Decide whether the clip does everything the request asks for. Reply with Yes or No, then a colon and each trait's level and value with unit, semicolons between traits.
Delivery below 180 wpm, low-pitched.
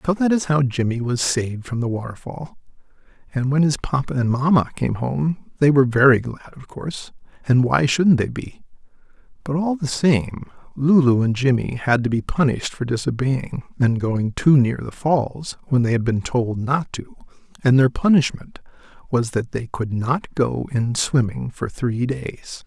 No: average, 185 wpm; low, 130 Hz